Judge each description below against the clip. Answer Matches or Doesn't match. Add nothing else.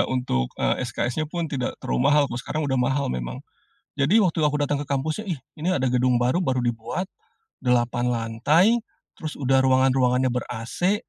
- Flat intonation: Doesn't match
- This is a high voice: Doesn't match